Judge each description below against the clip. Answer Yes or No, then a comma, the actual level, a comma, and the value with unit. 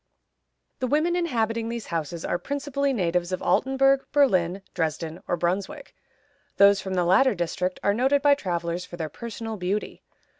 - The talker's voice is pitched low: No, high, 200 Hz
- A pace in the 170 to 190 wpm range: No, average, 155 wpm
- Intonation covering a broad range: Yes, wide, 7.3 semitones